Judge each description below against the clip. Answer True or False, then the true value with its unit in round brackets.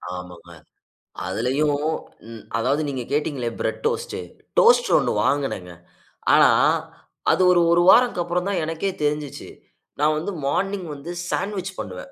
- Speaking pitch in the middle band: True (150 Hz)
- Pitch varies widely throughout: True (6.5 semitones)